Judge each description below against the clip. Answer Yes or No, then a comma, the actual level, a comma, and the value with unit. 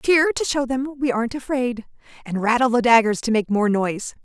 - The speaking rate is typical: No, fast, 210 wpm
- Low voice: No, high, 245 Hz